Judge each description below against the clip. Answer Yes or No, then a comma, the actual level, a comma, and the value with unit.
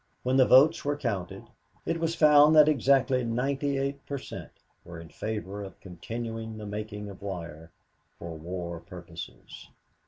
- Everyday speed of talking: Yes, average, 155 wpm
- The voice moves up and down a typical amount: No, wide, 7.2 semitones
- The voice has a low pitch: Yes, low, 110 Hz